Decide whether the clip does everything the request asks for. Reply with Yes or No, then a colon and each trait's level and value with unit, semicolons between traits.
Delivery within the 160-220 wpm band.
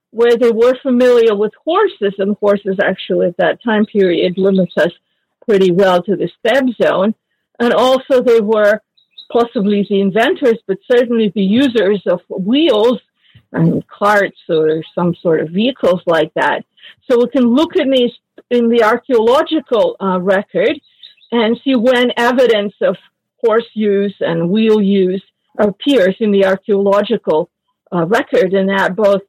No: average, 150 wpm